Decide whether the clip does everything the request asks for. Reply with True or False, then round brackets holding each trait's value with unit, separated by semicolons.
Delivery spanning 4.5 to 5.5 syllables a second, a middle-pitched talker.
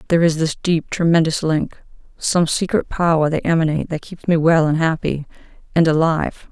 False (5.7 syllables/s; 160 Hz)